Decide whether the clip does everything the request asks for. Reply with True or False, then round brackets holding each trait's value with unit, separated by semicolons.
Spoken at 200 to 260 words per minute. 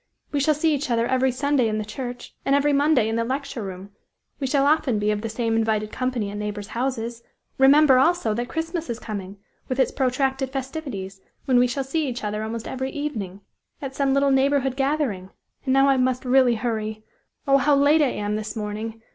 True (205 wpm)